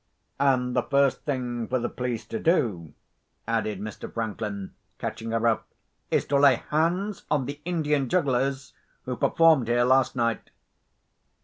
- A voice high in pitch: No, low, 125 Hz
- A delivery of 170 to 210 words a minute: No, average, 145 wpm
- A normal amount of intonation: Yes, average, 3.6 semitones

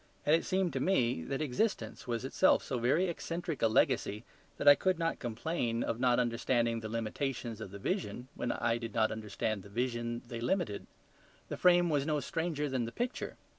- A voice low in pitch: Yes, low, 125 Hz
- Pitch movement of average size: No, wide, 5.9 semitones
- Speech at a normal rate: Yes, average, 195 wpm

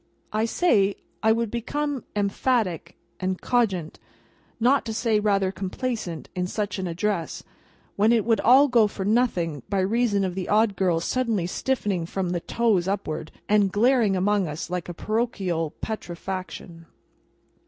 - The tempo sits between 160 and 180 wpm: No, average, 150 wpm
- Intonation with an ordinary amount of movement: Yes, average, 4.1 semitones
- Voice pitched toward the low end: No, high, 200 Hz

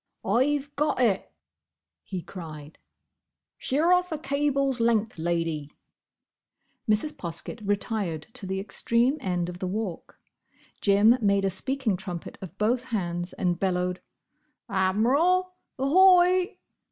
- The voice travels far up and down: Yes, wide, 7.1 semitones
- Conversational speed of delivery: No, slow, 115 wpm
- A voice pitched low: No, high, 210 Hz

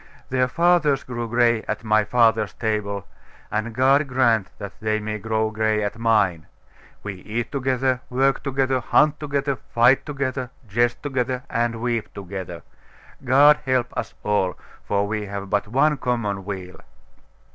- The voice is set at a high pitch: No, low, 115 Hz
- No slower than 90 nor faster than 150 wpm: Yes, average, 145 wpm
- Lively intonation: No, average, 3.7 semitones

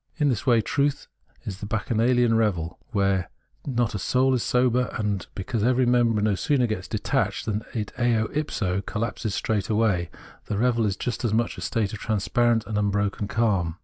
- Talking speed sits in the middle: Yes, average, 175 wpm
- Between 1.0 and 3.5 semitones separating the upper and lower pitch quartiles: Yes, average, 3.1 semitones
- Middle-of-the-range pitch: No, low, 110 Hz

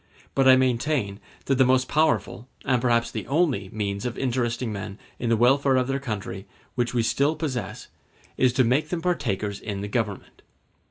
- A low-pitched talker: Yes, low, 125 Hz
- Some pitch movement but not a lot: Yes, average, 3.9 semitones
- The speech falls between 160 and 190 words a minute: Yes, average, 180 wpm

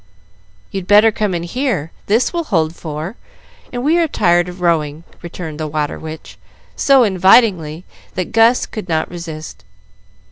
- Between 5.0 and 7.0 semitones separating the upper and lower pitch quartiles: Yes, wide, 5.6 semitones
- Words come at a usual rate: Yes, average, 150 wpm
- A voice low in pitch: No, medium, 180 Hz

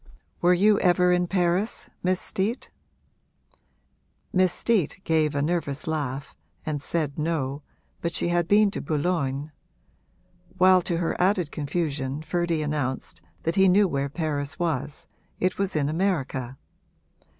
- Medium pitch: Yes, medium, 165 Hz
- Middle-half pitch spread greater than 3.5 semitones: Yes, average, 4.0 semitones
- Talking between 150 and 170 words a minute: No, slow, 135 wpm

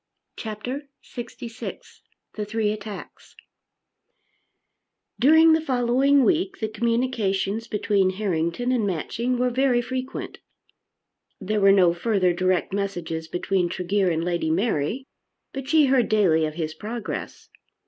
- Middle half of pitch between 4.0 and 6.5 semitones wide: Yes, average, 5.2 semitones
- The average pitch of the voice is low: No, high, 215 Hz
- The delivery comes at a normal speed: No, slow, 120 wpm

